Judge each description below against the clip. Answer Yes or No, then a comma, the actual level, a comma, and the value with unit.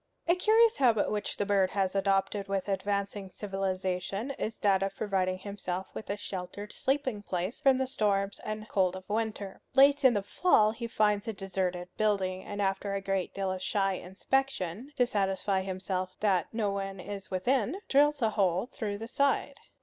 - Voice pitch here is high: Yes, high, 200 Hz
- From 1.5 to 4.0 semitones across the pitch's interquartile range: Yes, narrow, 2.6 semitones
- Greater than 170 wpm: Yes, average, 180 wpm